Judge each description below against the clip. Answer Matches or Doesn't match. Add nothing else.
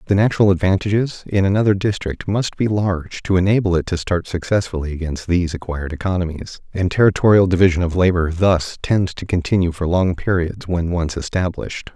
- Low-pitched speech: Matches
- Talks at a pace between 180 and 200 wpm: Doesn't match